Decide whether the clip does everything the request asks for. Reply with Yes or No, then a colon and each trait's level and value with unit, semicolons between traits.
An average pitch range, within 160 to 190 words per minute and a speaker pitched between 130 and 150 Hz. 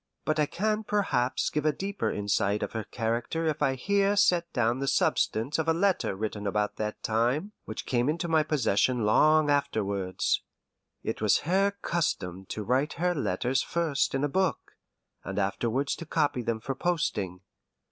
No: wide, 6.9 semitones; average, 170 wpm; low, 135 Hz